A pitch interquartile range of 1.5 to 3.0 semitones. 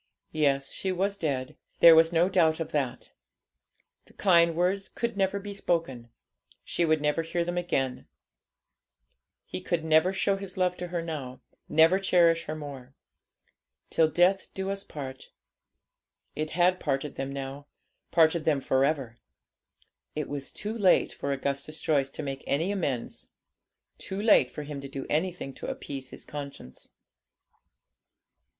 No: average, 4.5 semitones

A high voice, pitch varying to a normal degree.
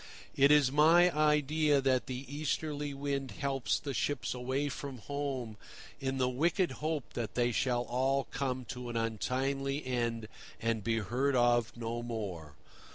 No: low, 130 Hz; average, 3.0 semitones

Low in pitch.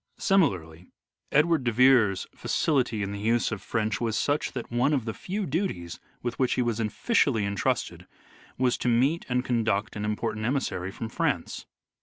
Yes: low, 120 Hz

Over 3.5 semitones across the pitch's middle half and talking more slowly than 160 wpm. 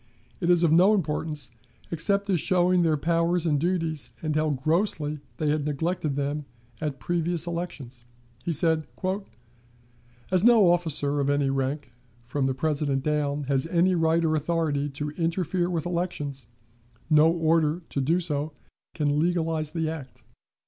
No: average, 2.8 semitones; average, 150 wpm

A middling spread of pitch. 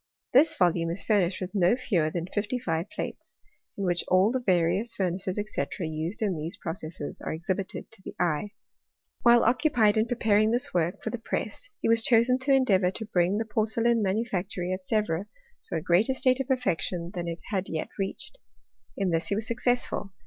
Yes: average, 4.7 semitones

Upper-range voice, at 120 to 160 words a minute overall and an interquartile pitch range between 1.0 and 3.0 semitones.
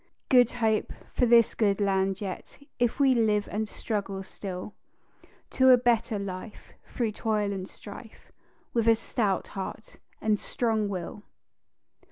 Yes: high, 215 Hz; average, 140 wpm; average, 2.7 semitones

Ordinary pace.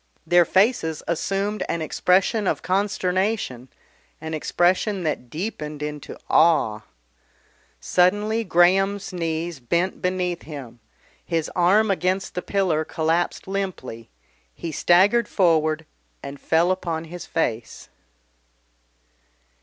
No: slow, 105 wpm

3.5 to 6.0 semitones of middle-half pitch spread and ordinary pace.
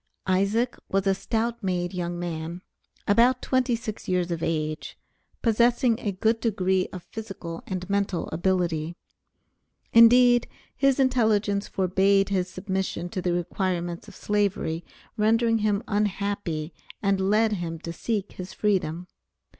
No: average, 3.8 semitones; slow, 130 wpm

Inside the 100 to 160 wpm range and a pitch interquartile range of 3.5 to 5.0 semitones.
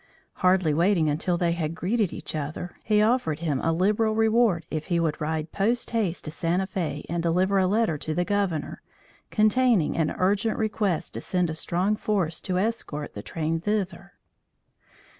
No: average, 175 wpm; average, 4.4 semitones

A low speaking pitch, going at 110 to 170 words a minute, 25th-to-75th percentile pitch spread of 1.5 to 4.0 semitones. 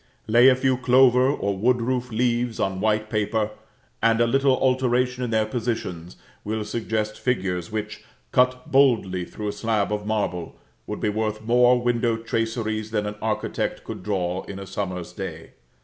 Yes: low, 110 Hz; average, 165 wpm; average, 2.9 semitones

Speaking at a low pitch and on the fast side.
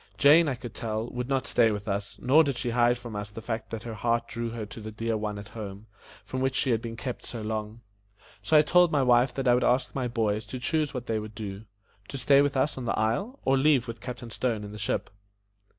Yes: low, 120 Hz; fast, 260 wpm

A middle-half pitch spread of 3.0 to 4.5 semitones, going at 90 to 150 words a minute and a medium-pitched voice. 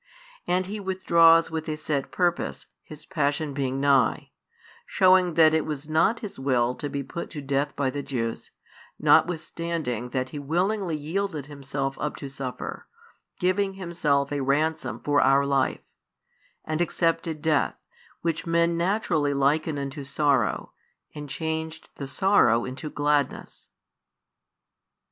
Yes: average, 3.3 semitones; slow, 135 wpm; medium, 150 Hz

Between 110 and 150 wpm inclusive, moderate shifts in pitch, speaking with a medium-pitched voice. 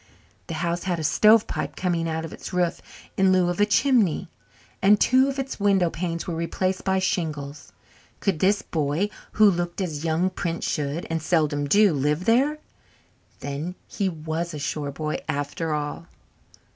No: average, 170 wpm; average, 3.7 semitones; medium, 170 Hz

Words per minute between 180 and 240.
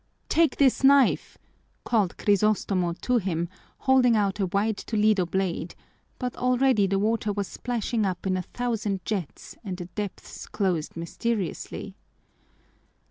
No: slow, 135 wpm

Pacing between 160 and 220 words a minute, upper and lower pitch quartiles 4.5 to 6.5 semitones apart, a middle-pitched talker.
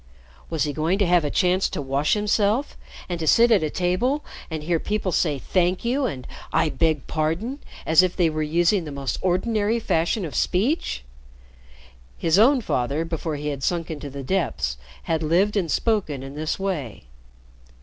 Yes: average, 180 wpm; average, 4.8 semitones; medium, 170 Hz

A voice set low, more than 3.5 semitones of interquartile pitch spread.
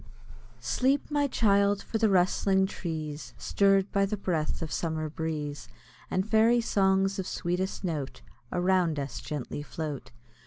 No: high, 190 Hz; average, 4.0 semitones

